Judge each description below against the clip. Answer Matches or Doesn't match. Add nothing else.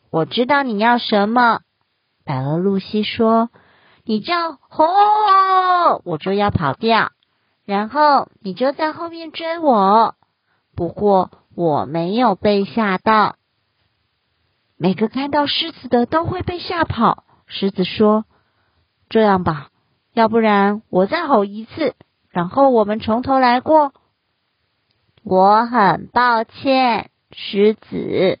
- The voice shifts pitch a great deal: Matches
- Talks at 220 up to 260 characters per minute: Doesn't match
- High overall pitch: Matches